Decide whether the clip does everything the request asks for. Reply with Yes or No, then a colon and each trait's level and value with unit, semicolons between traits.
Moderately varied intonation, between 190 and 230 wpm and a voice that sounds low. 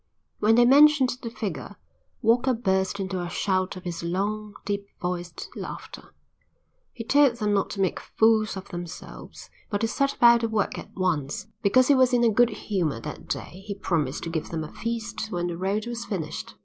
No: average, 4.4 semitones; average, 195 wpm; high, 205 Hz